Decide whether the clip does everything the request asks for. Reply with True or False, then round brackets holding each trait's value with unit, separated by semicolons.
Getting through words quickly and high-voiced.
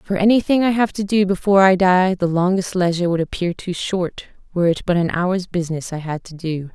False (230 wpm; 180 Hz)